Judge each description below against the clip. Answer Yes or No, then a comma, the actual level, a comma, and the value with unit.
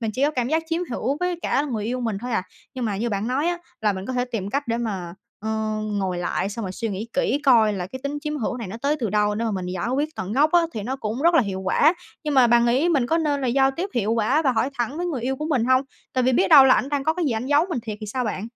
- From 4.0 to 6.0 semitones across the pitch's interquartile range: Yes, average, 4.8 semitones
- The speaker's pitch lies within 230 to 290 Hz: Yes, high, 245 Hz